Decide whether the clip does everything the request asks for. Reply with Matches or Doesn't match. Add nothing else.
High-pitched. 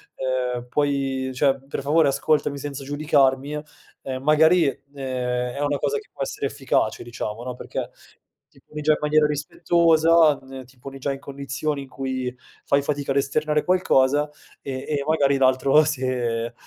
Doesn't match